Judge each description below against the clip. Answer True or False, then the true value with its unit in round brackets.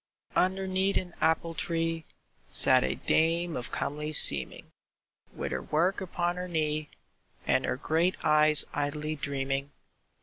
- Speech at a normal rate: False (130 wpm)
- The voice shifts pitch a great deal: False (2.7 semitones)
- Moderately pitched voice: True (160 Hz)